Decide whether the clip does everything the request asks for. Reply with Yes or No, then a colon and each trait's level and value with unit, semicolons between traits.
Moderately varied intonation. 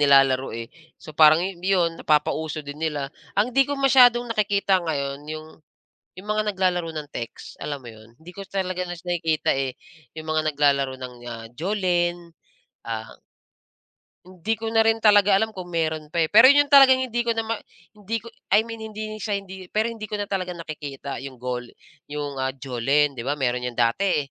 No: wide, 6.7 semitones